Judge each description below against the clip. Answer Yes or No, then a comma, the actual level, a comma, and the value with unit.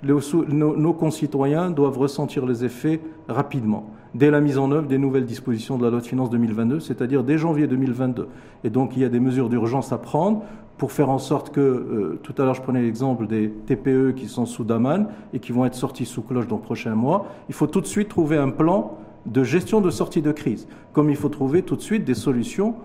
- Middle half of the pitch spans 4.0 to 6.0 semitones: No, average, 3.3 semitones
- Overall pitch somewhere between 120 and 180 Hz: Yes, low, 135 Hz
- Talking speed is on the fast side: Yes, fast, 225 wpm